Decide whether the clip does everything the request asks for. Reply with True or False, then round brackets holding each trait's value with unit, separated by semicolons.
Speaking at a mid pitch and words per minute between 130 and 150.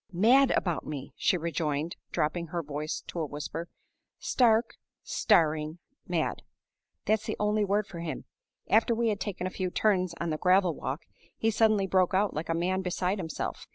False (180 Hz; 175 wpm)